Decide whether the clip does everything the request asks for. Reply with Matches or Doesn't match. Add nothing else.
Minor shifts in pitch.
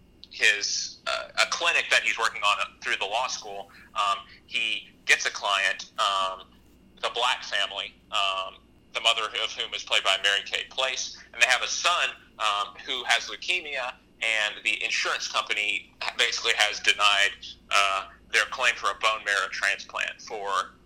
Matches